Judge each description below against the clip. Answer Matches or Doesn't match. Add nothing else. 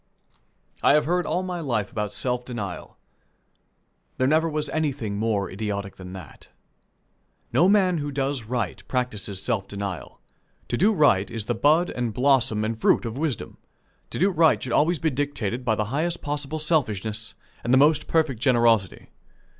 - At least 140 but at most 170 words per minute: Matches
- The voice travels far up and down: Matches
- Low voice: Matches